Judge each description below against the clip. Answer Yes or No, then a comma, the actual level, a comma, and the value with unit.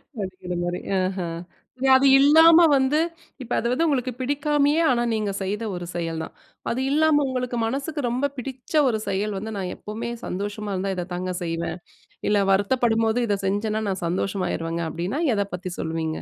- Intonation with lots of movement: Yes, wide, 6.1 semitones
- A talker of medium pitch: No, high, 210 Hz